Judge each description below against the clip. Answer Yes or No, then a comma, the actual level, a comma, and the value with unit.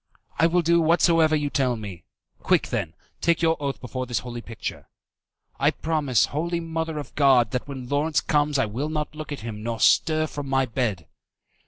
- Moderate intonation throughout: Yes, average, 4.3 semitones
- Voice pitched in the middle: Yes, medium, 145 Hz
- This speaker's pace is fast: No, average, 190 wpm